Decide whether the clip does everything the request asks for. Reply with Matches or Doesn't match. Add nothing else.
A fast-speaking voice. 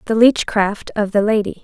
Doesn't match